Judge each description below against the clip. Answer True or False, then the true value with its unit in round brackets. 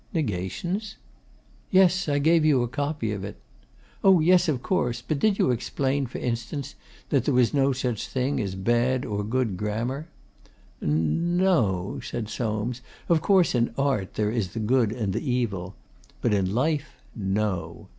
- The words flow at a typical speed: True (165 wpm)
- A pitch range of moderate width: False (5.7 semitones)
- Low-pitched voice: True (125 Hz)